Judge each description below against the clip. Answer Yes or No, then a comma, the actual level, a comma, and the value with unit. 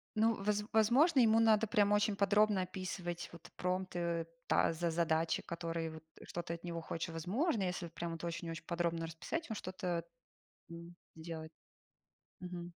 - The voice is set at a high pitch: No, medium, 175 Hz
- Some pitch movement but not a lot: Yes, average, 3.7 semitones